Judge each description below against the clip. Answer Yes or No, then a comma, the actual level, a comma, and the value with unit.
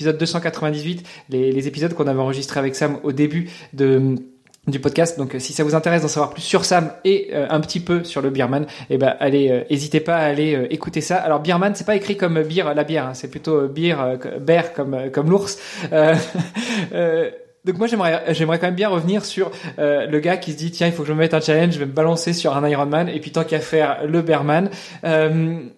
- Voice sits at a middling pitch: Yes, medium, 160 Hz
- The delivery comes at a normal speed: No, fast, 240 wpm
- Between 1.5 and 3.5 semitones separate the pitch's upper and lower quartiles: Yes, average, 2.8 semitones